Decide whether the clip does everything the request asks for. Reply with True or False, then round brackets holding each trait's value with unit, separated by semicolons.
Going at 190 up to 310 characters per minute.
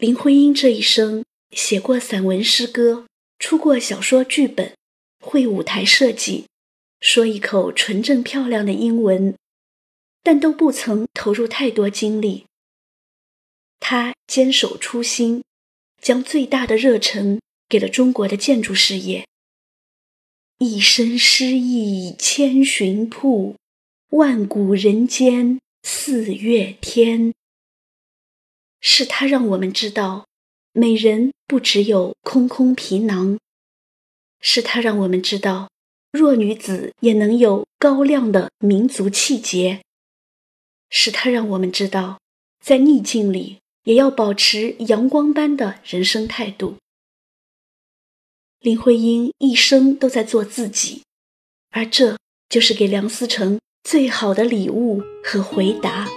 False (175 characters per minute)